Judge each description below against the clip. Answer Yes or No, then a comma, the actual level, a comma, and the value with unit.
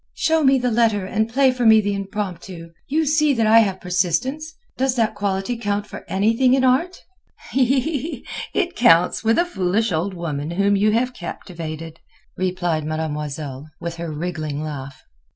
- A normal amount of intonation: No, wide, 6.9 semitones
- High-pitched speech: Yes, high, 200 Hz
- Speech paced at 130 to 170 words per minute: Yes, average, 160 wpm